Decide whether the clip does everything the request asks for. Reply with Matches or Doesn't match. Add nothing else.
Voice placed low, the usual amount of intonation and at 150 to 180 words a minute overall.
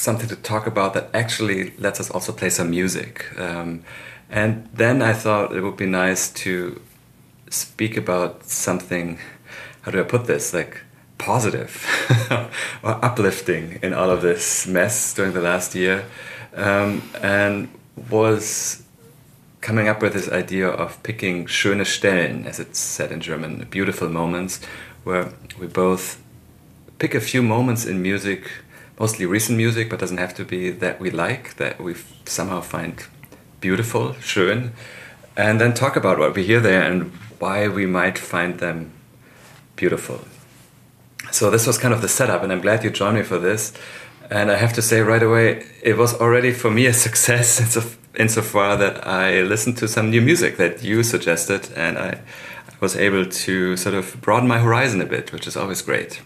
Matches